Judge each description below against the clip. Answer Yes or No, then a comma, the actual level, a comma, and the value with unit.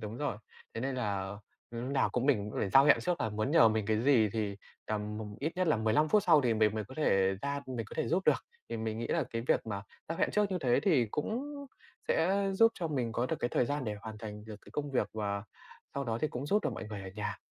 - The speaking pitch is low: Yes, low, 120 Hz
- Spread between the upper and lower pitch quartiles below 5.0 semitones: No, average, 5.3 semitones